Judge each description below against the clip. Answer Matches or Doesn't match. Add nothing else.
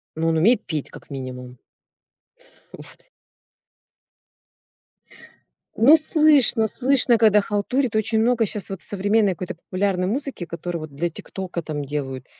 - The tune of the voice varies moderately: Doesn't match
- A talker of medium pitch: Doesn't match